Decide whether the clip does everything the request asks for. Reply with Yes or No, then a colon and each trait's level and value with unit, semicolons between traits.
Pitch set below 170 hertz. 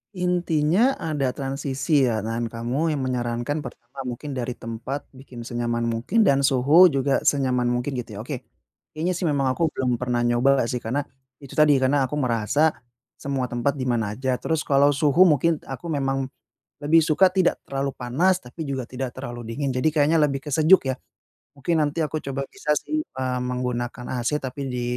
Yes: low, 135 Hz